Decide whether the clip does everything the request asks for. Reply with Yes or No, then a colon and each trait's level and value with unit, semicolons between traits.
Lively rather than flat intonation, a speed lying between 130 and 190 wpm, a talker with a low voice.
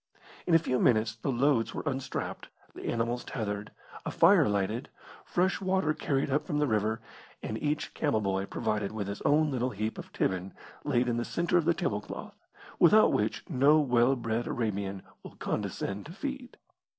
Yes: wide, 5.9 semitones; average, 180 wpm; low, 120 Hz